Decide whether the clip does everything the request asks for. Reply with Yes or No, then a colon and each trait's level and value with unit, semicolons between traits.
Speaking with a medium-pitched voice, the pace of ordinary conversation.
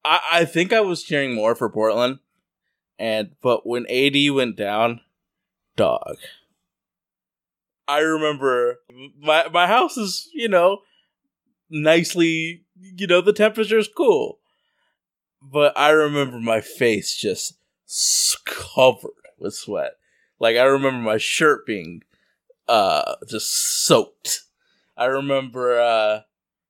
No: medium, 150 Hz; slow, 115 wpm